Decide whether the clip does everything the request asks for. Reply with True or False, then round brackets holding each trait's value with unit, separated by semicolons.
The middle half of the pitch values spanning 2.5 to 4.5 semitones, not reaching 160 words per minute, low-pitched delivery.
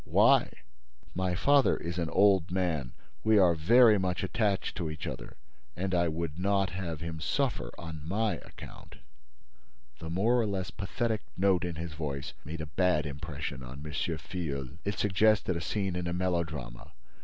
False (3.8 semitones; 165 wpm; 90 Hz)